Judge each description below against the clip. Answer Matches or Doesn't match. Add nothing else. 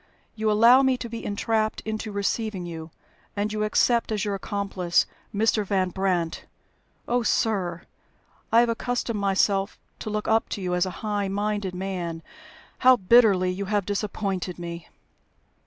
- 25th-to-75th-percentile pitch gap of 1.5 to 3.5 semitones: Matches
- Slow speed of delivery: Doesn't match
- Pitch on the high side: Matches